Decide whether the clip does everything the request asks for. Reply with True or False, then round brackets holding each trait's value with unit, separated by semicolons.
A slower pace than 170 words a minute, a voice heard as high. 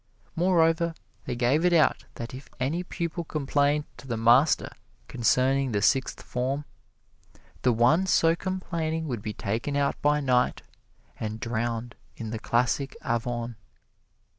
False (140 wpm; 135 Hz)